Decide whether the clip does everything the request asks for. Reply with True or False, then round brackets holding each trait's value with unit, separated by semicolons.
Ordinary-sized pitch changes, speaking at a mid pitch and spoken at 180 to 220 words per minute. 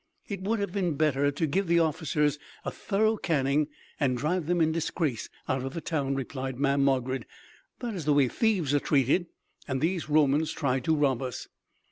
True (3.9 semitones; 150 Hz; 190 wpm)